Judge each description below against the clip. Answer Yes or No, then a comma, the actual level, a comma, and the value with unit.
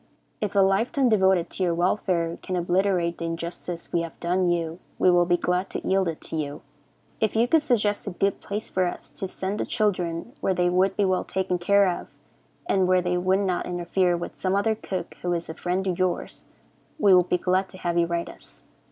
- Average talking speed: No, fast, 225 wpm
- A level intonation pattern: Yes, narrow, 1.9 semitones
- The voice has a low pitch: No, medium, 185 Hz